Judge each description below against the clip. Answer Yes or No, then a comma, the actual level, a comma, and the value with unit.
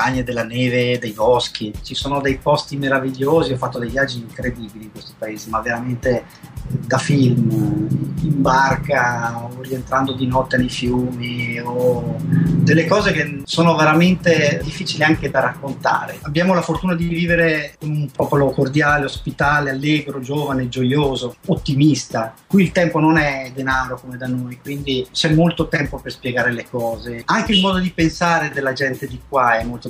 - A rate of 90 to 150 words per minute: No, average, 165 wpm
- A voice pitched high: No, low, 135 Hz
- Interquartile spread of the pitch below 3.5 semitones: No, average, 3.8 semitones